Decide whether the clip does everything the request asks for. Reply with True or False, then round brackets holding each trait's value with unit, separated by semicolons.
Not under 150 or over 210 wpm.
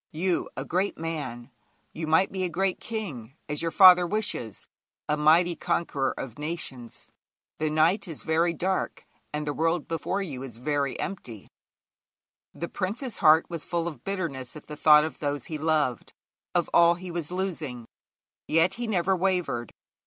True (165 wpm)